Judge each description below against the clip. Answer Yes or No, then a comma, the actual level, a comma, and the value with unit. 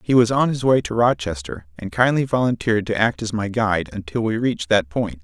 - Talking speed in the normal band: No, fast, 230 wpm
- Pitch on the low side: Yes, low, 105 Hz